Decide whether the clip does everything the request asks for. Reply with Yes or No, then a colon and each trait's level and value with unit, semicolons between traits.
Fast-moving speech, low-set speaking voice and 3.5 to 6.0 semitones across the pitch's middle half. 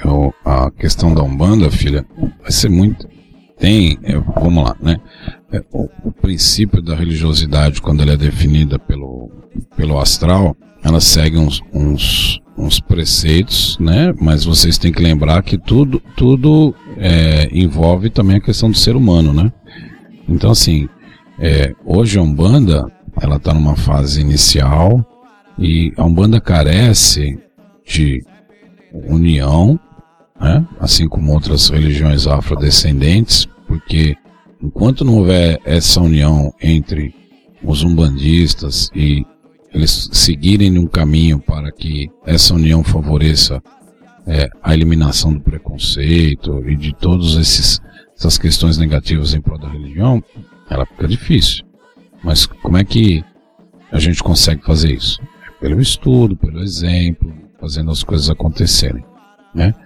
No: average, 130 wpm; very low, 80 Hz; average, 3.9 semitones